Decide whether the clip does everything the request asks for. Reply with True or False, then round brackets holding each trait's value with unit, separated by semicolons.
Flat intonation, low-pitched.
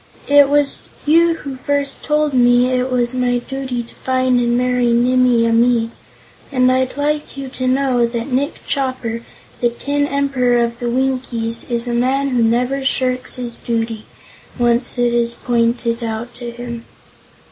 False (2.0 semitones; 250 Hz)